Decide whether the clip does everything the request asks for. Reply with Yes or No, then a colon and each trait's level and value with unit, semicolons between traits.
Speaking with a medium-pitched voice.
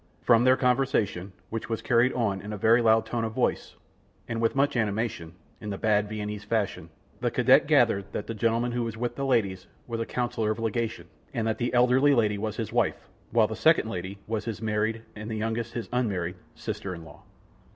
No: low, 110 Hz